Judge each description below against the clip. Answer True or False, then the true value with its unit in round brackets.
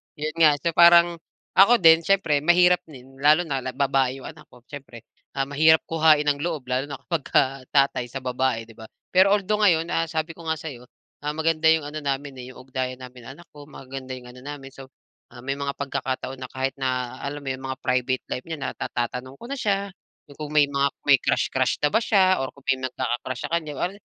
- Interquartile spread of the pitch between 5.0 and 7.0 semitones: False (3.6 semitones)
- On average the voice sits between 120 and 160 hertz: True (140 Hz)